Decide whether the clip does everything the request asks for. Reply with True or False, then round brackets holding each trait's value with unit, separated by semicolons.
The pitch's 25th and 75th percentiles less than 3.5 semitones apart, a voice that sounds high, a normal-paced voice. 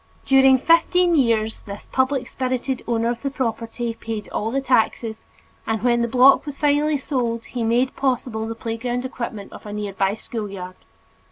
True (3.0 semitones; 240 Hz; 170 wpm)